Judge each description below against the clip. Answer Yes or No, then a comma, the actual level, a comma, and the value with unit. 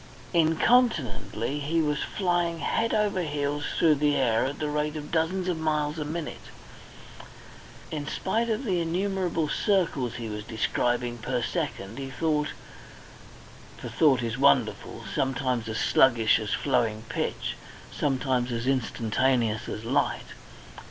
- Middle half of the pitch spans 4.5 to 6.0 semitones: Yes, average, 5.2 semitones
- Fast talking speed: No, slow, 135 wpm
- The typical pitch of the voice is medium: Yes, medium, 145 Hz